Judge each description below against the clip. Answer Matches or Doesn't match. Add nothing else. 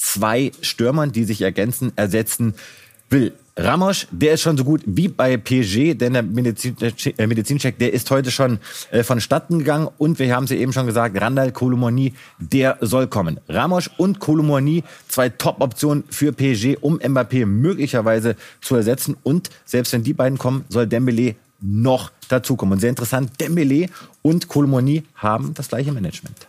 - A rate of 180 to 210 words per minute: Doesn't match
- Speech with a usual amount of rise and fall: Matches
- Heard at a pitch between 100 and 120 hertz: Doesn't match